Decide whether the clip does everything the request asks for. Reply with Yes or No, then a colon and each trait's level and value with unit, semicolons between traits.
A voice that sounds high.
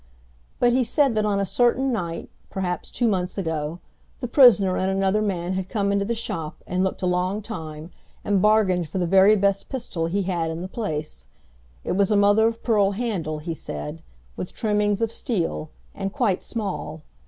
Yes: high, 195 Hz